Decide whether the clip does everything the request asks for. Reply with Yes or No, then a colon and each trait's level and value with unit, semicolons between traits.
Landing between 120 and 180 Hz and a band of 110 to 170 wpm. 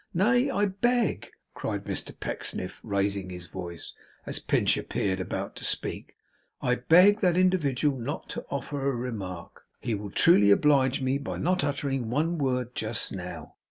Yes: low, 135 Hz; average, 160 wpm